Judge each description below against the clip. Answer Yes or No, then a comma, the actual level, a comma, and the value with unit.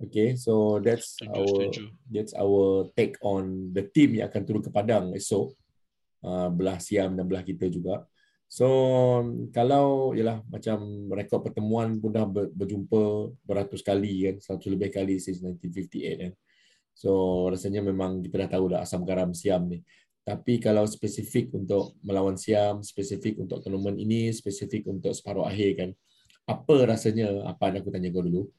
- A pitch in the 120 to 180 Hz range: No, low, 100 Hz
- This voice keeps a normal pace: No, fast, 160 wpm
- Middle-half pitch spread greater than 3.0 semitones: No, narrow, 2.6 semitones